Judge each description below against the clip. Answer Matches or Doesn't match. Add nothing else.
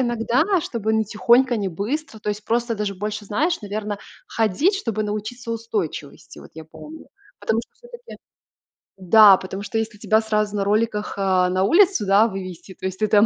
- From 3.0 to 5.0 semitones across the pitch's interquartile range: Doesn't match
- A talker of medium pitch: Doesn't match